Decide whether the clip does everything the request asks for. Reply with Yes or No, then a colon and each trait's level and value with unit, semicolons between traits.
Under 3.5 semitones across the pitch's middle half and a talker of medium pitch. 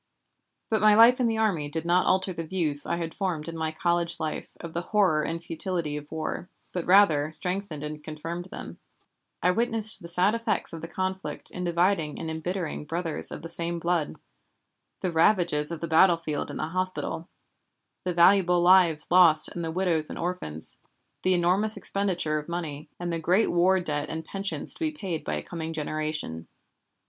Yes: average, 2.8 semitones; medium, 170 Hz